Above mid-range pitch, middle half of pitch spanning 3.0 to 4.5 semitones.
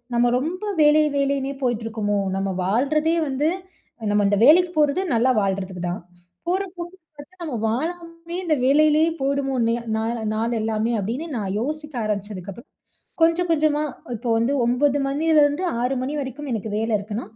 No: very high, 270 Hz; wide, 5.5 semitones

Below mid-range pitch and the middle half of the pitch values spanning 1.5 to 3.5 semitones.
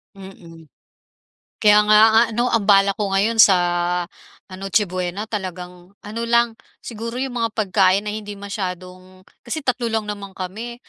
No: high, 200 Hz; average, 3.1 semitones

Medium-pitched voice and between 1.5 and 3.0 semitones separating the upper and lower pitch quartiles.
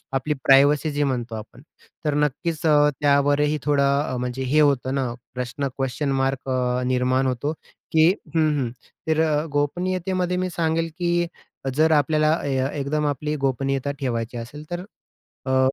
Yes: medium, 145 Hz; average, 2.7 semitones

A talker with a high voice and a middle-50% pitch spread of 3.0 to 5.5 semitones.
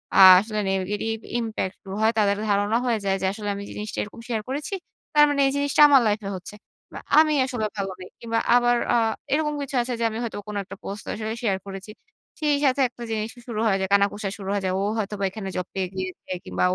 Yes: high, 215 Hz; average, 3.3 semitones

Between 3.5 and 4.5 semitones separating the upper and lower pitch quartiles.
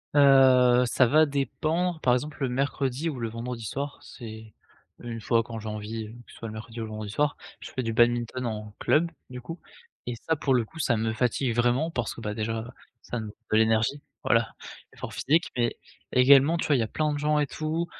Yes: average, 4.2 semitones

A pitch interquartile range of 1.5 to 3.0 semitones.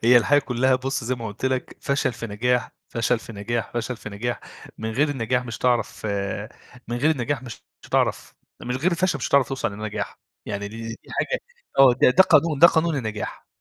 No: average, 3.5 semitones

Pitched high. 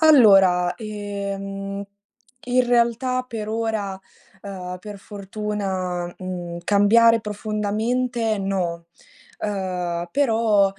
Yes: high, 205 Hz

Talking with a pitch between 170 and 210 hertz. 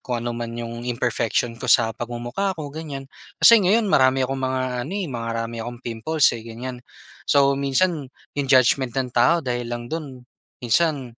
No: low, 130 Hz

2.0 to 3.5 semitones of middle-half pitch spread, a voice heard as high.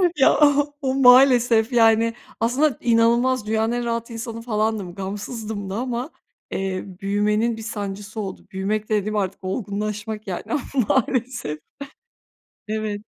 Yes: average, 2.8 semitones; high, 220 Hz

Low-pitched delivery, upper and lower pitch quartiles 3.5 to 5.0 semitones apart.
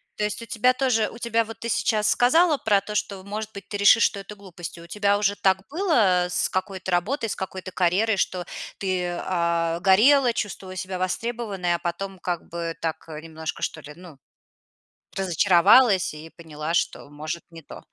No: high, 190 Hz; average, 3.8 semitones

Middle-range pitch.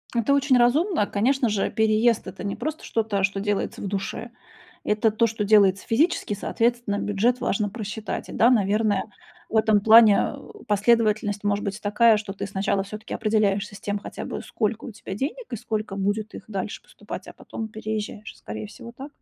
No: high, 215 Hz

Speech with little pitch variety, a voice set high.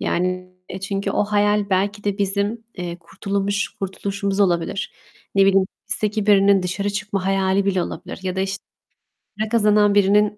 Yes: narrow, 1.4 semitones; high, 200 Hz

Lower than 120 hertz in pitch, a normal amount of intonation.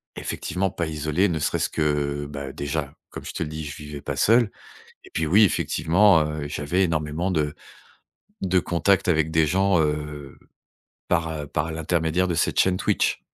Yes: very low, 80 Hz; average, 3.1 semitones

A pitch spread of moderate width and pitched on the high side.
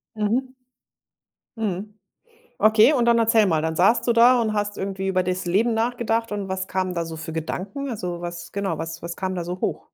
Yes: average, 4.2 semitones; high, 195 Hz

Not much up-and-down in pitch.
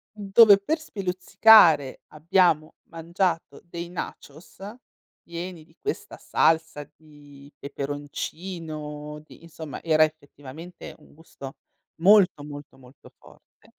No: average, 3.5 semitones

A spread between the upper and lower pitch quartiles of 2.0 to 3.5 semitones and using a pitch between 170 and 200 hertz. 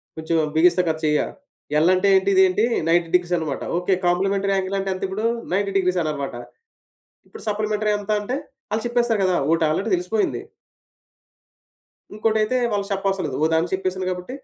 Yes: average, 2.8 semitones; high, 190 Hz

